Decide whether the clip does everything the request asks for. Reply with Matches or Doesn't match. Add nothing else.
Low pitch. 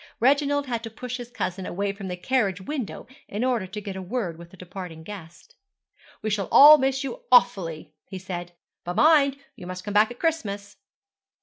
Doesn't match